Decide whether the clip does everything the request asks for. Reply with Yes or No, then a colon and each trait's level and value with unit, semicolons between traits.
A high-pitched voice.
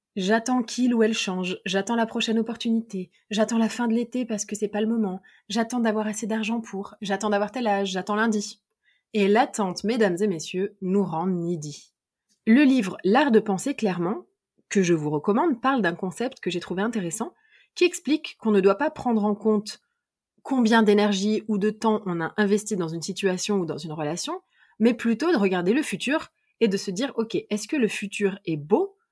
Yes: high, 215 Hz